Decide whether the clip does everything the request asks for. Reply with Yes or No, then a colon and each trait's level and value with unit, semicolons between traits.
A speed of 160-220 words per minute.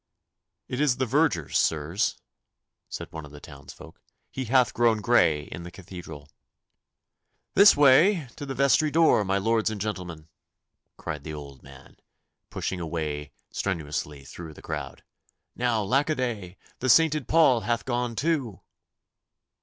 No: average, 145 wpm